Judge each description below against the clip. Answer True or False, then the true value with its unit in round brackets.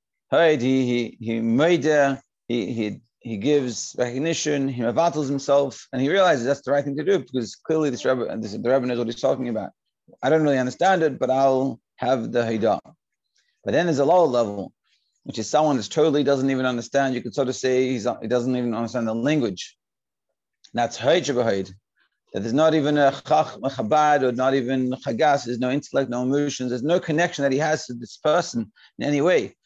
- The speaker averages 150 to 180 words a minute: False (190 wpm)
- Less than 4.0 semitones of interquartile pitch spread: True (3.3 semitones)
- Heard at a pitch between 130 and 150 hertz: True (135 Hz)